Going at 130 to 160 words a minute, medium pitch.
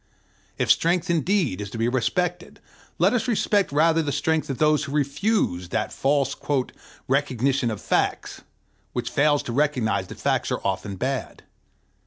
Yes: average, 155 wpm; medium, 145 Hz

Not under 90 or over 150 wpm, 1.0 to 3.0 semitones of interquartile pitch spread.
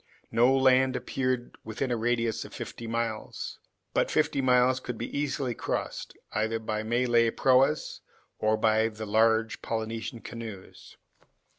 Yes: slow, 135 wpm; narrow, 2.4 semitones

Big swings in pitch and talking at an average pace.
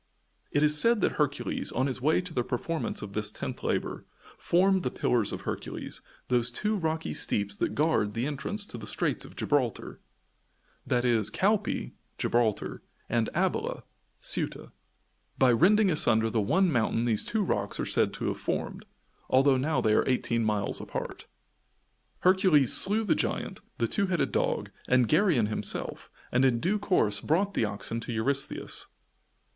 Yes: wide, 7.7 semitones; average, 160 wpm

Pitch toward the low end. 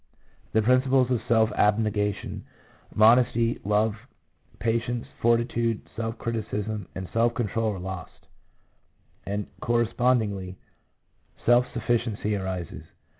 Yes: low, 115 Hz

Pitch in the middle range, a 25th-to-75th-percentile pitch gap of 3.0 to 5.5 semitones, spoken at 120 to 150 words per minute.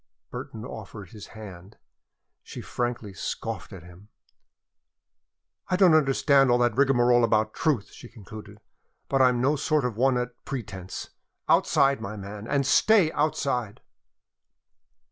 No: low, 120 Hz; average, 4.5 semitones; slow, 135 wpm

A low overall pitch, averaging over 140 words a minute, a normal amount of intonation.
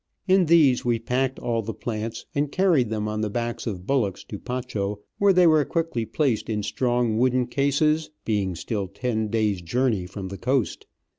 Yes: low, 120 Hz; average, 180 wpm; average, 4.3 semitones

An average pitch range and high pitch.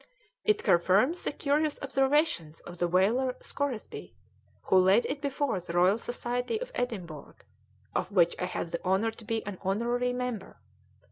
No: wide, 6.4 semitones; high, 225 Hz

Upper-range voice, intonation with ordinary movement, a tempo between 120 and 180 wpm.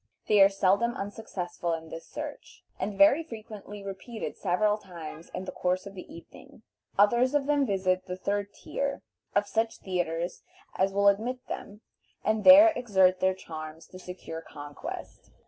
Yes: high, 200 Hz; average, 3.5 semitones; average, 165 wpm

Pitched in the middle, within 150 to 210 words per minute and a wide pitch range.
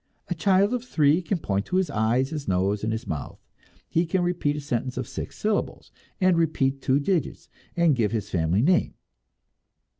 Yes: medium, 145 Hz; average, 185 wpm; wide, 7.8 semitones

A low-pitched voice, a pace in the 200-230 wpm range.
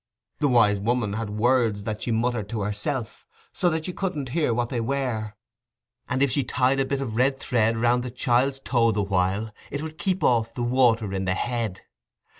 Yes: low, 120 Hz; fast, 205 wpm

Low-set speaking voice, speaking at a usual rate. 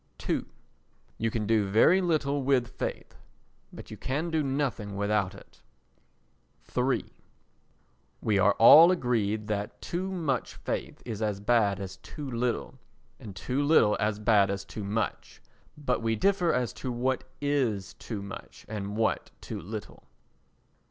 Yes: low, 115 Hz; average, 145 wpm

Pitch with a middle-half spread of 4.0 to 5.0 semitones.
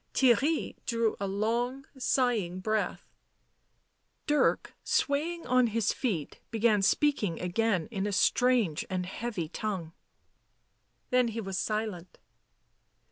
Yes: average, 4.6 semitones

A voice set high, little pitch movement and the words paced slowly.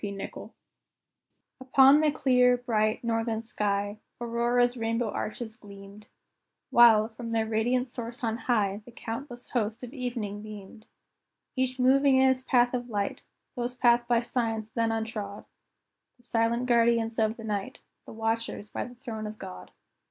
No: high, 230 Hz; narrow, 2.2 semitones; average, 150 wpm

